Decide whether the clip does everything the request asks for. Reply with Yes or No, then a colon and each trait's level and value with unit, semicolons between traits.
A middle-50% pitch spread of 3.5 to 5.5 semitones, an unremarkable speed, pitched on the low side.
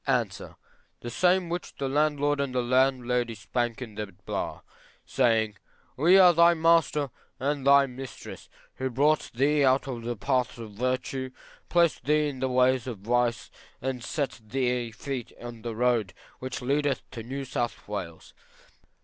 No: average, 3.0 semitones; average, 155 wpm; low, 130 Hz